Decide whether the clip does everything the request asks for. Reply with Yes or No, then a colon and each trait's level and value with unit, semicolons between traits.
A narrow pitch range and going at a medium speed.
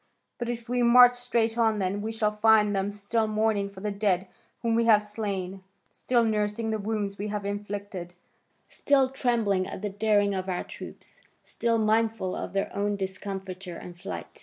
Yes: narrow, 2.3 semitones; average, 180 wpm